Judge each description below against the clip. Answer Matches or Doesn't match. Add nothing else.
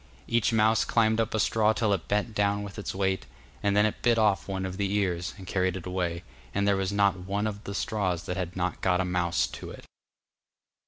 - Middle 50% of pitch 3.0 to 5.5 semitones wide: Doesn't match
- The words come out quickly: Matches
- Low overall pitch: Matches